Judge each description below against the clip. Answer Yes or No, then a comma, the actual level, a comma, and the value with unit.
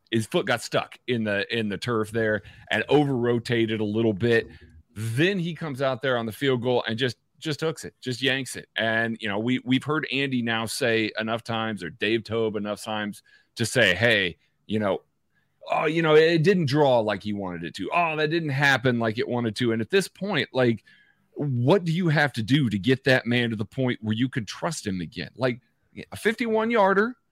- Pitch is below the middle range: Yes, low, 120 Hz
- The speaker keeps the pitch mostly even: No, average, 4.5 semitones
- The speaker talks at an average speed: No, fast, 220 wpm